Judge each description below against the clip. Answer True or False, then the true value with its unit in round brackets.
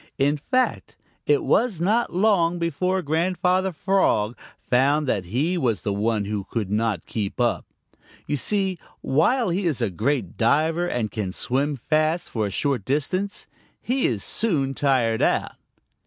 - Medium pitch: True (145 Hz)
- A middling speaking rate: True (155 wpm)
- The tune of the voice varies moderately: False (8.0 semitones)